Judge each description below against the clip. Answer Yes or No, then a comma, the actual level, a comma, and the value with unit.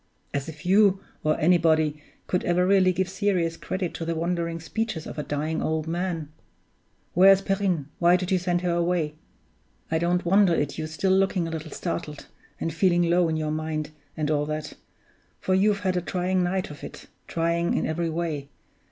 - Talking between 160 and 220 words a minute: Yes, average, 190 wpm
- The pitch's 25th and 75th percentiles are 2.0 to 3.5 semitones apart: Yes, average, 2.7 semitones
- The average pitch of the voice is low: No, medium, 170 Hz